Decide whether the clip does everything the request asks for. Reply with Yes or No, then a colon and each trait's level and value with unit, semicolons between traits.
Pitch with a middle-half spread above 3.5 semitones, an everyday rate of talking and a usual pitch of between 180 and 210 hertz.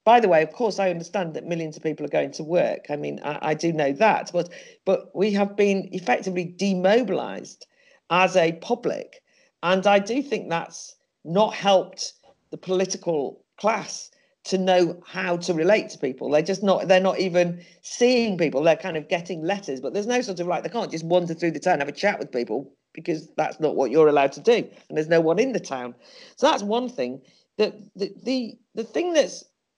No: average, 4.0 semitones; fast, 215 wpm; medium, 185 Hz